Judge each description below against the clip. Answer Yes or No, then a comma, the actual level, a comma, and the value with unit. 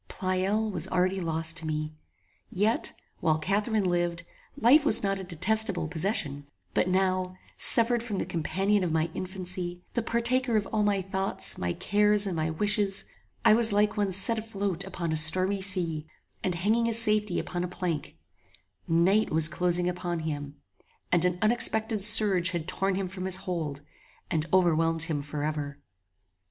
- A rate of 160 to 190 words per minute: Yes, average, 165 wpm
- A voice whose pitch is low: No, medium, 185 Hz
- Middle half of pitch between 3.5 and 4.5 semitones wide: Yes, average, 4.0 semitones